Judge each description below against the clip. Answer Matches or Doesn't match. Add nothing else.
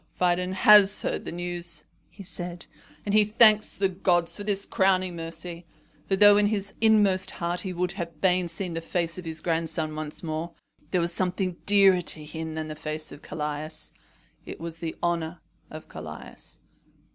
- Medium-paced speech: Matches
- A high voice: Doesn't match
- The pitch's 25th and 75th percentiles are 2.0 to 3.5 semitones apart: Matches